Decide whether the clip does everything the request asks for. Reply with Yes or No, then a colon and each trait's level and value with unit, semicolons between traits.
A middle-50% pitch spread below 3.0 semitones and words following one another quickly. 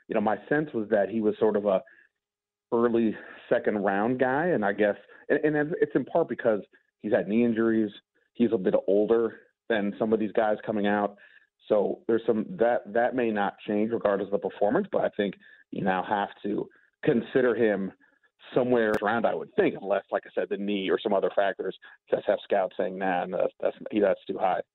Yes: narrow, 2.5 semitones; fast, 210 wpm